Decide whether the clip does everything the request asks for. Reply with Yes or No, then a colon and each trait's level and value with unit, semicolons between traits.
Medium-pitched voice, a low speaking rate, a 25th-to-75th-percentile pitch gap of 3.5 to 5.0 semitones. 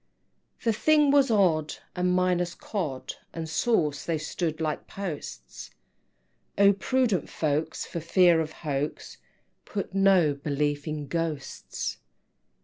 Yes: medium, 170 Hz; slow, 125 wpm; average, 4.5 semitones